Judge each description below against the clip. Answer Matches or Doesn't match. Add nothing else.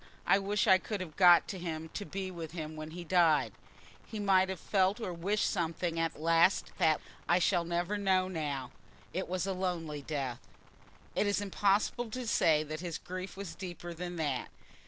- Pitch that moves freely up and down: Doesn't match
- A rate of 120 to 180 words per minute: Doesn't match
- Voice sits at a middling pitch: Matches